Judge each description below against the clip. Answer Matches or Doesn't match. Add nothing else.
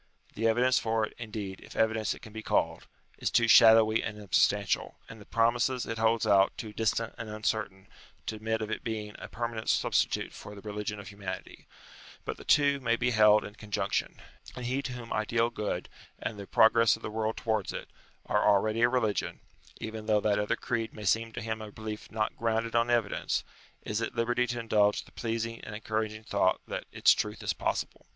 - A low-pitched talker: Matches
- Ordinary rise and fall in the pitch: Doesn't match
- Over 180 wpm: Matches